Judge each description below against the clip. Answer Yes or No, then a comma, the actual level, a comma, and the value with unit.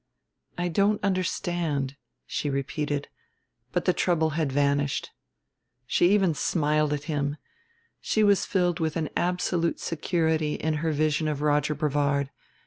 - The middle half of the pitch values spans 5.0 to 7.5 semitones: No, average, 3.1 semitones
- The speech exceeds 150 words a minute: No, slow, 135 wpm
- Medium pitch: Yes, medium, 155 Hz